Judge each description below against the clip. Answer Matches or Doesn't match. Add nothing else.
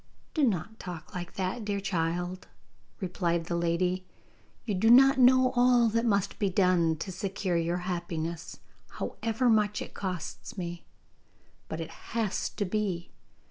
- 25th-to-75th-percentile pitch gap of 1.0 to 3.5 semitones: Doesn't match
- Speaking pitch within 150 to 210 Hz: Matches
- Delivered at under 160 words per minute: Matches